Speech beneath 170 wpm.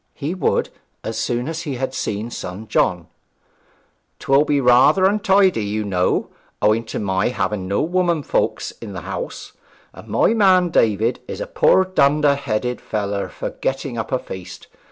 Yes: average, 160 wpm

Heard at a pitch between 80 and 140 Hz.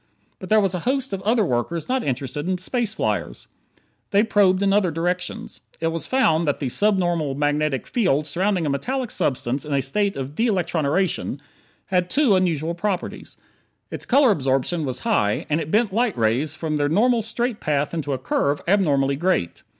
No: medium, 170 Hz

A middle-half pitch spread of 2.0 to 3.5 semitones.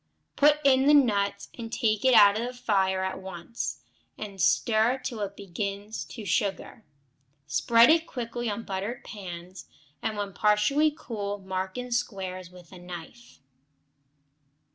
No: average, 4.0 semitones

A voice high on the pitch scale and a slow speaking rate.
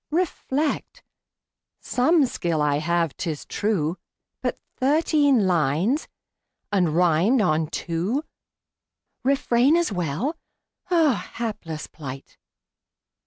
Yes: high, 200 Hz; slow, 90 wpm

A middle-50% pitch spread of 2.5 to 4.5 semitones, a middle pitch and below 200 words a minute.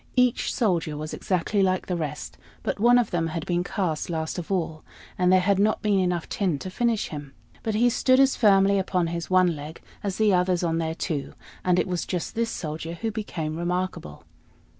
No: average, 3.6 semitones; medium, 180 Hz; fast, 205 wpm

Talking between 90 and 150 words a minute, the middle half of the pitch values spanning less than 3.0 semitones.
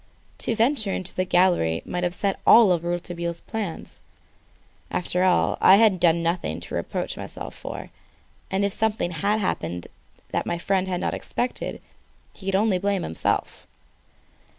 Yes: average, 145 wpm; narrow, 2.6 semitones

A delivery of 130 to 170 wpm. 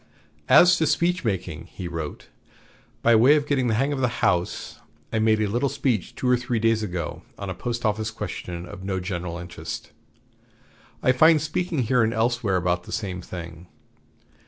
No: average, 180 wpm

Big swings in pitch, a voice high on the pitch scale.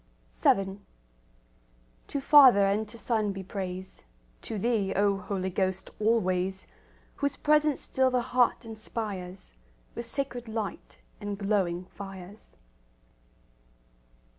No: average, 3.7 semitones; high, 205 Hz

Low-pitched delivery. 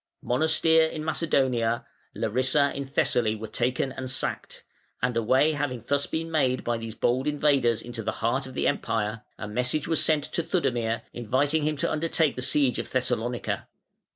Yes: low, 130 Hz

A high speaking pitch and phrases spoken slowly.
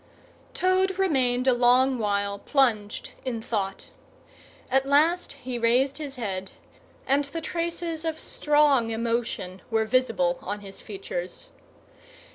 Yes: very high, 255 Hz; slow, 120 wpm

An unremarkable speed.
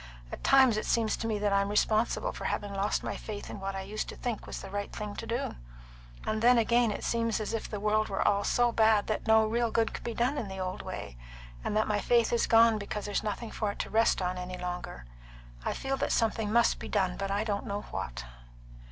No: fast, 245 wpm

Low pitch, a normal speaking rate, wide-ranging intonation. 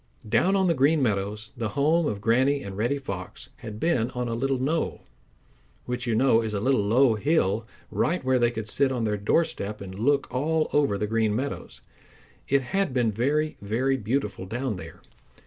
No: low, 125 Hz; average, 190 wpm; average, 4.7 semitones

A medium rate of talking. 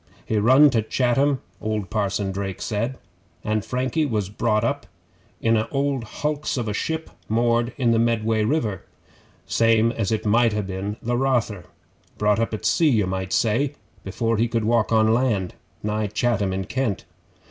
Yes: average, 170 wpm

